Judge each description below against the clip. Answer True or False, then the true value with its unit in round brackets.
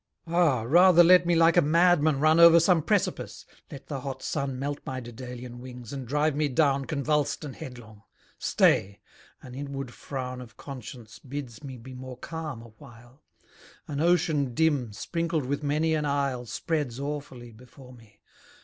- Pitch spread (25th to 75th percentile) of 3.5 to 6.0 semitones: True (3.8 semitones)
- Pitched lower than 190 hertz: True (140 Hz)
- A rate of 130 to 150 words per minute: False (160 wpm)